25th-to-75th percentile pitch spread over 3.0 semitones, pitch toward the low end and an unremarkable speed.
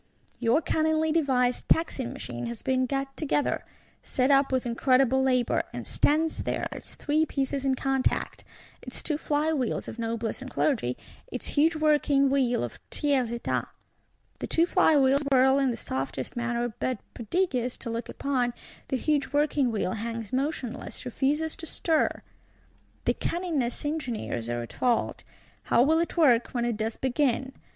No: average, 3.8 semitones; very high, 265 Hz; average, 160 wpm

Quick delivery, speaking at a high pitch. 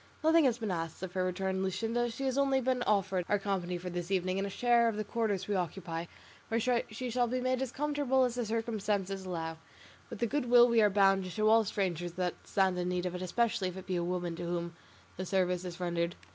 Yes: fast, 240 wpm; high, 195 Hz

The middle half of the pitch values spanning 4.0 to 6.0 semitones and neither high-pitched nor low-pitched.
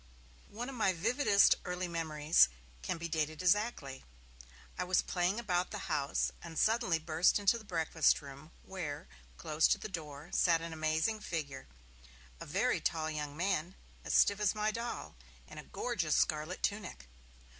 Yes: average, 4.6 semitones; medium, 170 Hz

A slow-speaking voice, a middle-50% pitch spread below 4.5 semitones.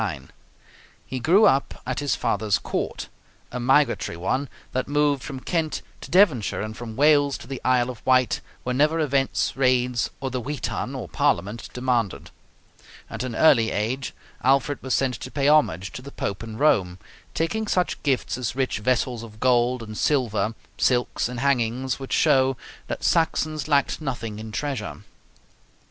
No: average, 160 wpm; average, 3.3 semitones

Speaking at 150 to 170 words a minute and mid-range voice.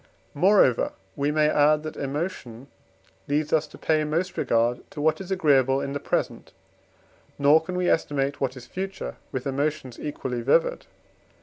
Yes: average, 160 wpm; medium, 145 Hz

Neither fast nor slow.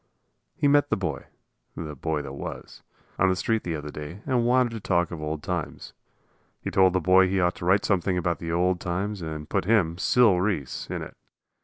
No: fast, 210 wpm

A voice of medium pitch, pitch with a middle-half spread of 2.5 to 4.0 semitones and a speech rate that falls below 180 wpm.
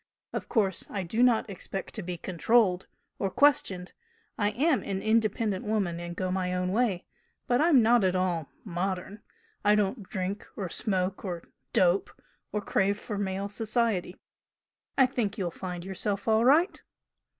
No: high, 200 Hz; average, 3.4 semitones; average, 160 wpm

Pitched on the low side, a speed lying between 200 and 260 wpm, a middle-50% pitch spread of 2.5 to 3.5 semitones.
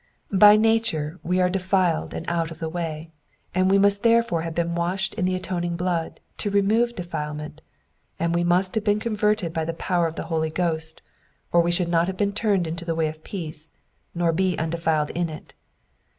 No: medium, 175 Hz; fast, 205 wpm; average, 2.9 semitones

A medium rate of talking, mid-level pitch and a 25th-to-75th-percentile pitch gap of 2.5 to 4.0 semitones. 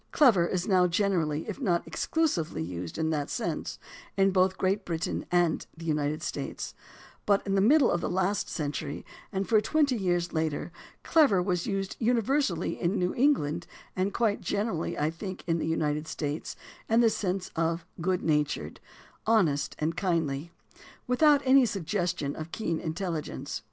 No: average, 165 wpm; medium, 180 Hz; average, 4.4 semitones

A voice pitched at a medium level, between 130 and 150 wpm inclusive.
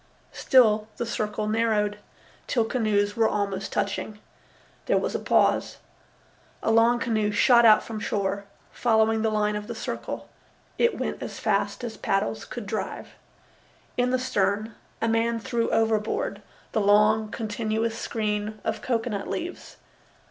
No: high, 220 Hz; average, 140 wpm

